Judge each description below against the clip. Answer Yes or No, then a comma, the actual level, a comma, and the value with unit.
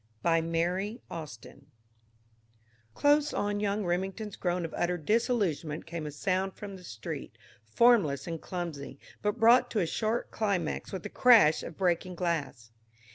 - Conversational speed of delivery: Yes, average, 145 wpm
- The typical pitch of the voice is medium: Yes, medium, 180 Hz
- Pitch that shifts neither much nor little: Yes, average, 4.3 semitones